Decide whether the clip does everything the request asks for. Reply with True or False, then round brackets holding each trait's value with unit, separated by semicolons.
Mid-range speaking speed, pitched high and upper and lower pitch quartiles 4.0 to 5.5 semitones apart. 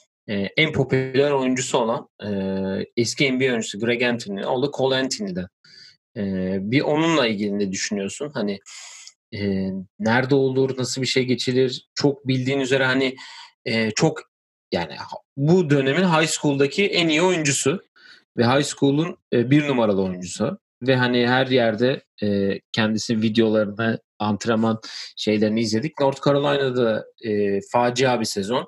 False (130 wpm; 125 Hz; 4.4 semitones)